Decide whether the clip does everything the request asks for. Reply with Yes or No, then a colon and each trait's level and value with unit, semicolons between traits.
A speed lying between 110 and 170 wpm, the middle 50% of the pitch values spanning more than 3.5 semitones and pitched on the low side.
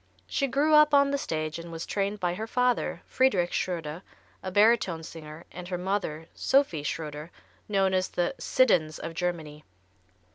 No: average, 160 wpm; wide, 5.6 semitones; medium, 180 Hz